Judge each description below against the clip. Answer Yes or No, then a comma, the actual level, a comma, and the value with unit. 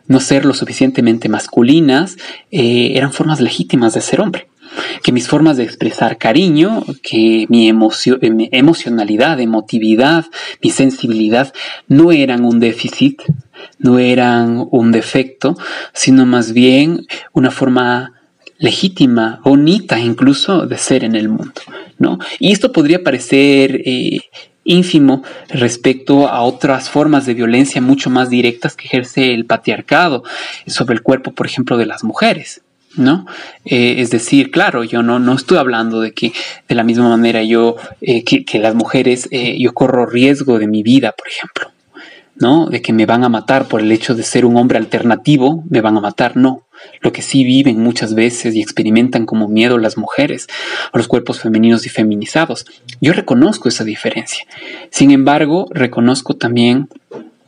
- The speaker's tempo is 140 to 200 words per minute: Yes, average, 160 wpm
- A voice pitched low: Yes, low, 125 Hz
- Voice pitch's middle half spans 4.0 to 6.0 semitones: No, average, 2.7 semitones